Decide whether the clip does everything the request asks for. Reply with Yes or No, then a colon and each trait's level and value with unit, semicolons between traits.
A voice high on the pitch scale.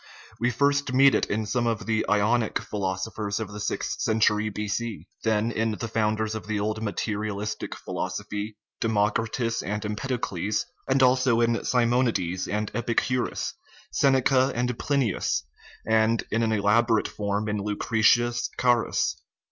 No: low, 110 Hz